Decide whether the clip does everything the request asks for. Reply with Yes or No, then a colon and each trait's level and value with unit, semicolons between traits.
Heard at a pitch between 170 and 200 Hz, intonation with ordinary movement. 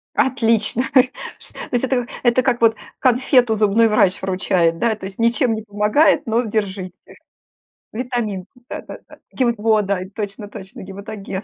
No: high, 220 Hz; average, 3.3 semitones